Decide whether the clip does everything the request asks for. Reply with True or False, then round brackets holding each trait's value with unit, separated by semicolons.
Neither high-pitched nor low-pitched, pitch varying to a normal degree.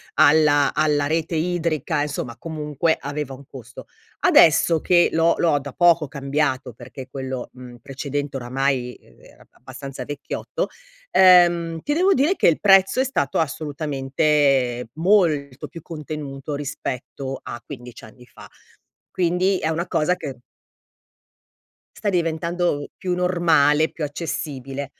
True (150 Hz; 3.7 semitones)